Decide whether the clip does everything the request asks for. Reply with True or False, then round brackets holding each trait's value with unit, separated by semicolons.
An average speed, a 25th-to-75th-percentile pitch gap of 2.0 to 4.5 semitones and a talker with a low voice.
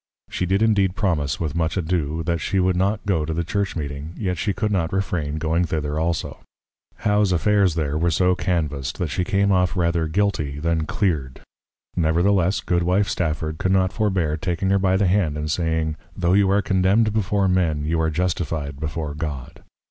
True (185 wpm; 3.5 semitones; 85 Hz)